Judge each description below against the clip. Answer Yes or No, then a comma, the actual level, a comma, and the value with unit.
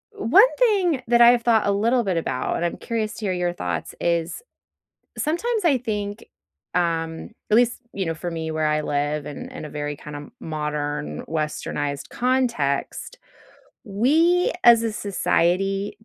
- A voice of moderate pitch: No, high, 195 Hz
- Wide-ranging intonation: Yes, wide, 7.6 semitones